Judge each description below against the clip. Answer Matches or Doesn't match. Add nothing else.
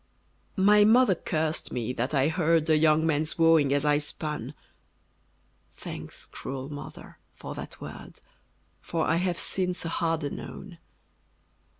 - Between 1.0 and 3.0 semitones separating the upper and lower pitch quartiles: Matches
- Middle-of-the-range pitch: Matches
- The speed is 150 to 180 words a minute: Doesn't match